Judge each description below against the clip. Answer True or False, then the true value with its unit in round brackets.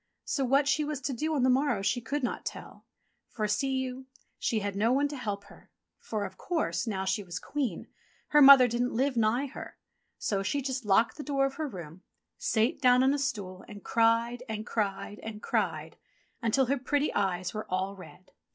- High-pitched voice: True (235 Hz)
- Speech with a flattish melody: False (5.1 semitones)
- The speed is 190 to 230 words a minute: True (205 wpm)